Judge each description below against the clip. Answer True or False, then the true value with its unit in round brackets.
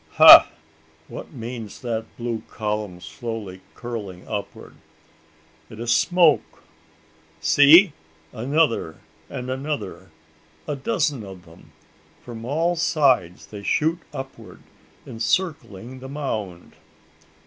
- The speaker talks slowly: True (100 wpm)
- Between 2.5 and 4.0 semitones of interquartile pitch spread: False (5.5 semitones)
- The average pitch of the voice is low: True (120 Hz)